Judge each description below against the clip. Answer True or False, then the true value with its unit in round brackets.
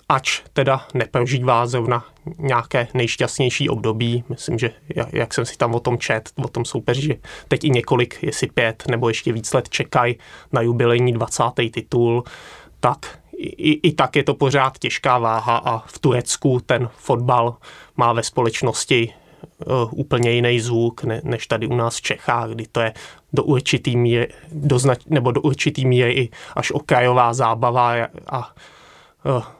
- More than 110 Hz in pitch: True (125 Hz)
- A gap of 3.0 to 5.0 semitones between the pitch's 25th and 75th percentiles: False (2.5 semitones)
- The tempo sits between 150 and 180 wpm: True (160 wpm)